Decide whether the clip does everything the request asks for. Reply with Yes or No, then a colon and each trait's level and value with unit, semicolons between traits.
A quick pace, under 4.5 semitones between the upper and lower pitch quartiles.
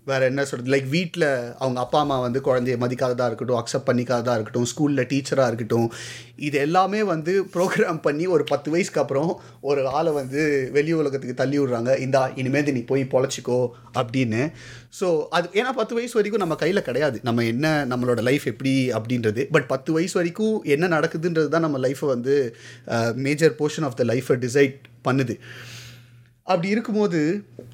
Yes: fast, 160 wpm; average, 4.1 semitones